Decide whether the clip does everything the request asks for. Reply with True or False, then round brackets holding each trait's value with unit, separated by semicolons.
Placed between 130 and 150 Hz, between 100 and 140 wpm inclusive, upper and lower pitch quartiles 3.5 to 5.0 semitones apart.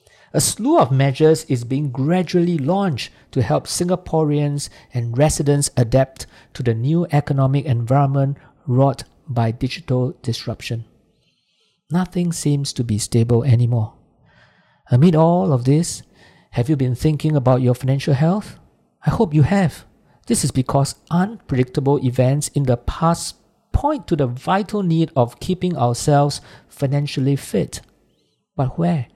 True (140 Hz; 135 wpm; 4.3 semitones)